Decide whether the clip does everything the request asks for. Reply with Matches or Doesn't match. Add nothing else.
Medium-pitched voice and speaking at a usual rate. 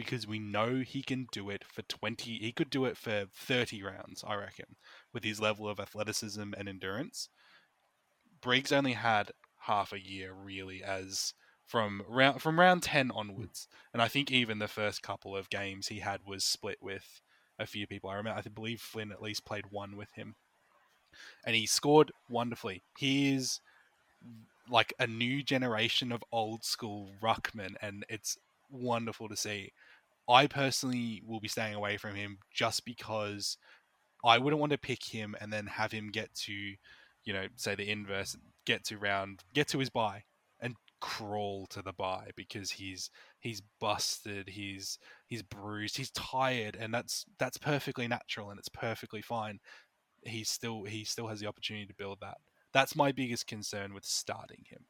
Doesn't match